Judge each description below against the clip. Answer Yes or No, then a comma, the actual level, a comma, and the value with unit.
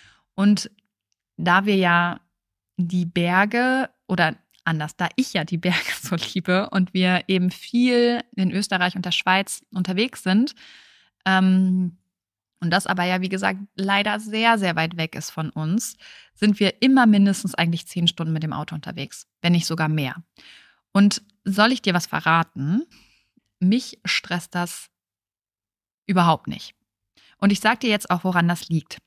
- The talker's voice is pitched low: No, medium, 185 Hz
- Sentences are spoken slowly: No, average, 155 wpm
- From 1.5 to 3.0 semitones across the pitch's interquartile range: No, average, 3.6 semitones